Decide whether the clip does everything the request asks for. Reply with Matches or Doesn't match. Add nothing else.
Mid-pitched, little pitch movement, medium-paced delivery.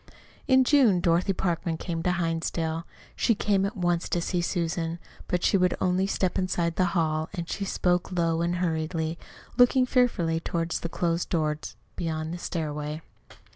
Matches